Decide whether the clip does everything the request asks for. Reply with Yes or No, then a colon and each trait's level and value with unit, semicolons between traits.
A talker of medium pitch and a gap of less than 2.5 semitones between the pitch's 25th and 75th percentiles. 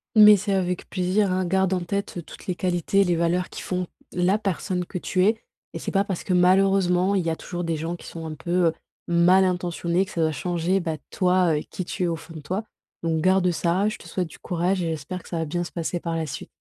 Yes: medium, 180 Hz; narrow, 2.0 semitones